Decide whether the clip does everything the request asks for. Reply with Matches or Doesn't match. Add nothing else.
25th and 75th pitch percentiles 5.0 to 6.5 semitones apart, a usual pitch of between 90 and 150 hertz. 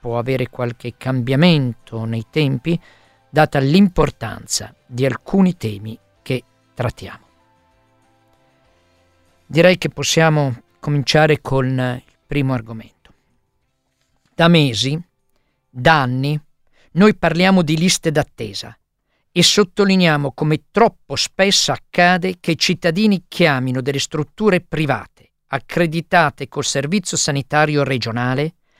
Matches